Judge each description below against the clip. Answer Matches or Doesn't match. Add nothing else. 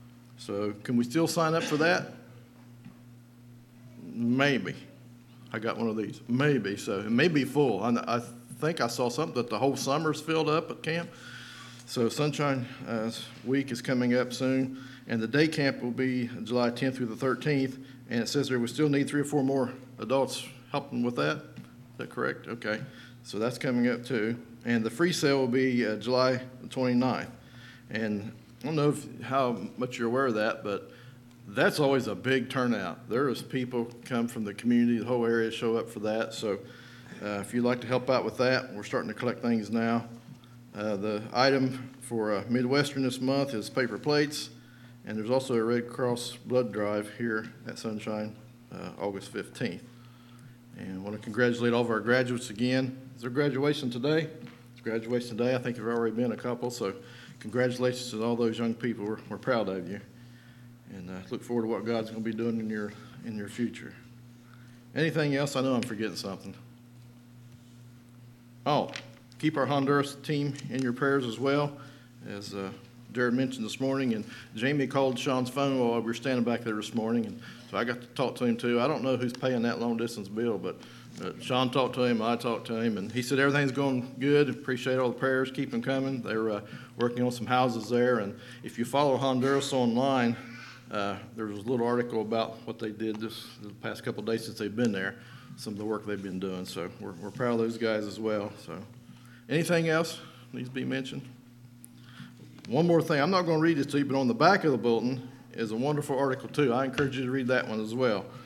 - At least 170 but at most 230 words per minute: Matches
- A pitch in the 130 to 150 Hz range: Doesn't match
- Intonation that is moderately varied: Doesn't match